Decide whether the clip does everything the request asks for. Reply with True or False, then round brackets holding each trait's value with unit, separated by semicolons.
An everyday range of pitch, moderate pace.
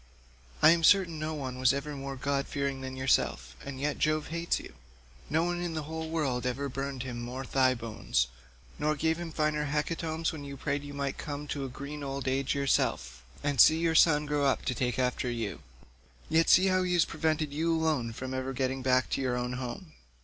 False (3.3 semitones; 215 wpm)